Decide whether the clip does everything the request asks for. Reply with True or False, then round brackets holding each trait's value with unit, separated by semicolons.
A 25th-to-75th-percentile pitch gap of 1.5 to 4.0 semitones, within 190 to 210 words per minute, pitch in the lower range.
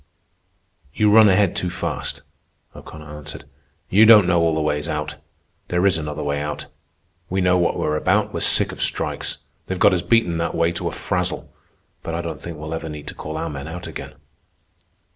True (3.1 semitones; 200 wpm; 85 Hz)